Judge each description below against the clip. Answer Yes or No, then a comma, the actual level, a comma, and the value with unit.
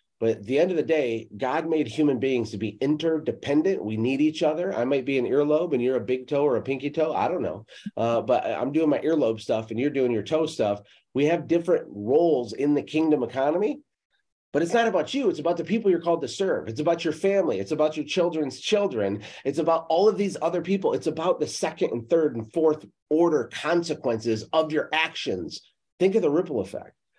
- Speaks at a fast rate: Yes, fast, 225 wpm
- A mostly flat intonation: No, average, 4.6 semitones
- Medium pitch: Yes, medium, 150 Hz